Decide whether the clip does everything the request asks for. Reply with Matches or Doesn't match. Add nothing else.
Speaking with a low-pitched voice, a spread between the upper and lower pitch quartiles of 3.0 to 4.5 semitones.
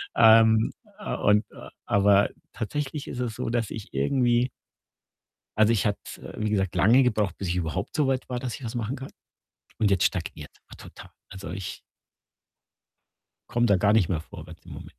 Matches